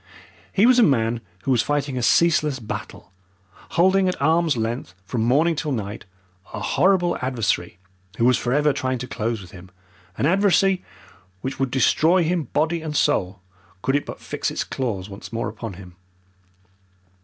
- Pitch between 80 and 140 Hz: Yes, low, 135 Hz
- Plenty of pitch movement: Yes, wide, 6.4 semitones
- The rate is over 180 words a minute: No, average, 165 wpm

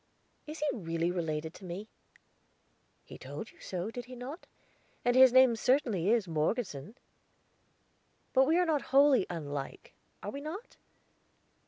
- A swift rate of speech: No, average, 140 wpm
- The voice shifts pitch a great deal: Yes, wide, 7.9 semitones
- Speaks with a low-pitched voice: No, high, 235 Hz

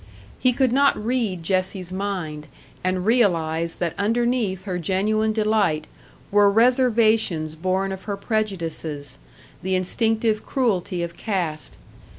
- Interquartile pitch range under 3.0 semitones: No, average, 4.0 semitones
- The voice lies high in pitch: Yes, high, 195 Hz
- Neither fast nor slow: No, slow, 120 wpm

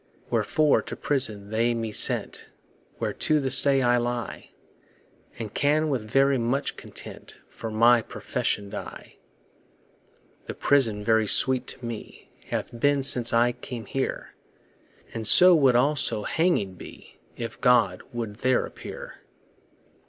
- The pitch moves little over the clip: No, average, 3.4 semitones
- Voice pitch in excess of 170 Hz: No, low, 120 Hz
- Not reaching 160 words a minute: Yes, slow, 135 wpm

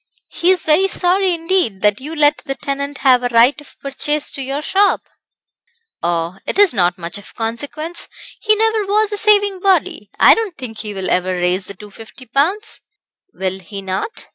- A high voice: Yes, very high, 280 Hz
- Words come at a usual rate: Yes, average, 185 wpm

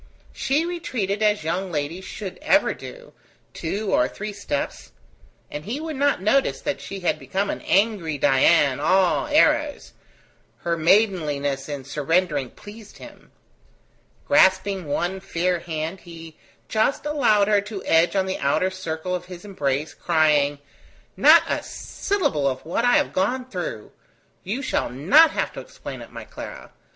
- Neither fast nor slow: Yes, average, 150 wpm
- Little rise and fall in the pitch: No, wide, 5.6 semitones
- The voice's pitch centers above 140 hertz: Yes, high, 190 Hz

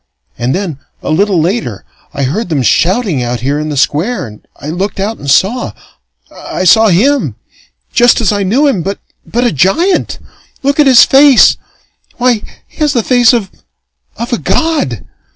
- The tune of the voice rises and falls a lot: Yes, wide, 8.1 semitones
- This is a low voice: No, high, 200 Hz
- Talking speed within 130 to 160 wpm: No, average, 170 wpm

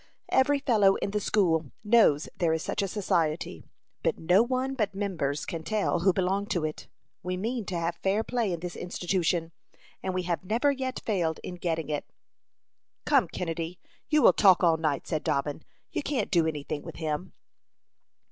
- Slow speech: No, average, 185 wpm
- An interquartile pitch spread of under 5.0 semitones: Yes, average, 4.3 semitones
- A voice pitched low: No, medium, 180 Hz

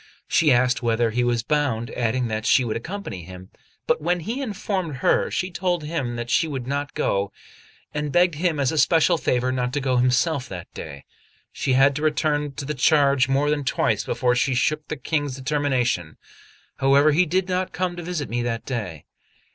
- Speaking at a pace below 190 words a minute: No, average, 195 wpm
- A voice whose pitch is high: No, medium, 140 Hz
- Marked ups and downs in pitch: No, average, 4.4 semitones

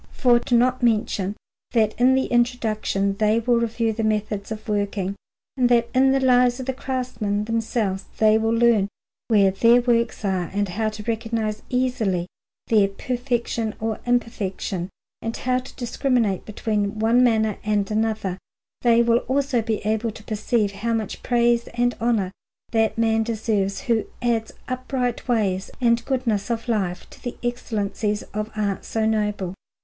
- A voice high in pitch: Yes, high, 225 Hz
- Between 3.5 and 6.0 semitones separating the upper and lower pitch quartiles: No, narrow, 2.5 semitones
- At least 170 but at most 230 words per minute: No, average, 155 wpm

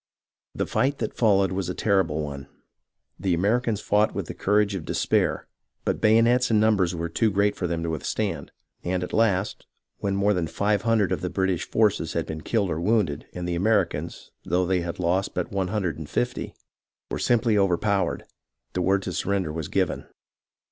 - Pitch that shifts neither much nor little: Yes, average, 3.6 semitones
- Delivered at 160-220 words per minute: Yes, average, 190 wpm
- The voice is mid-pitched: No, very low, 95 Hz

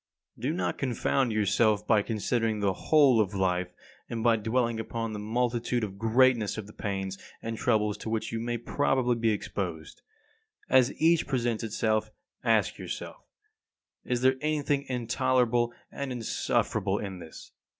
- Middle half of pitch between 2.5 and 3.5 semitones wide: Yes, average, 2.9 semitones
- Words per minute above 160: No, average, 150 wpm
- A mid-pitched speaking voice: No, low, 115 Hz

